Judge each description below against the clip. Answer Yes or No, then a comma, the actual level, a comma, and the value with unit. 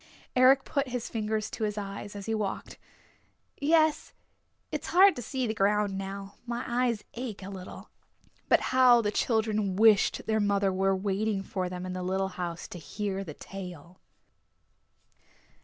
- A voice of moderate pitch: No, high, 205 Hz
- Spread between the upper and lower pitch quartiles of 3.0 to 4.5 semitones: Yes, average, 3.3 semitones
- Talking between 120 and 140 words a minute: No, average, 160 wpm